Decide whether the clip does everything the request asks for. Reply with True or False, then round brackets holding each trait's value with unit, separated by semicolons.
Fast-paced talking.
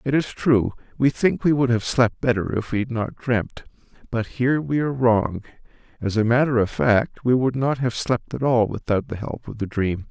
True (225 wpm)